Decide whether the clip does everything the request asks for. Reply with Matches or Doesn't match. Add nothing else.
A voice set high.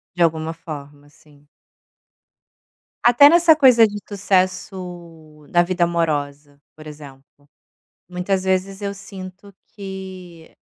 Doesn't match